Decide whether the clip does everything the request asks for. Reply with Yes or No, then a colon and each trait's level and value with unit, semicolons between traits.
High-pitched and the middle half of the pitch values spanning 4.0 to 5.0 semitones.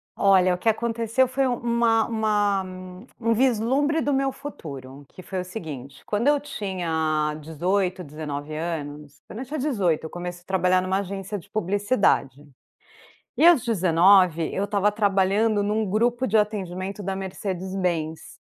Yes: high, 195 Hz; average, 4.6 semitones